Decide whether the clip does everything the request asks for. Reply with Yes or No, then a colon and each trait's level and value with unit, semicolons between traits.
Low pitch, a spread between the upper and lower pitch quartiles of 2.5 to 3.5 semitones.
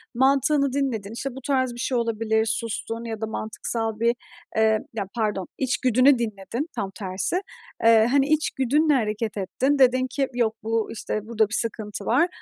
No: high, 230 Hz; average, 3.2 semitones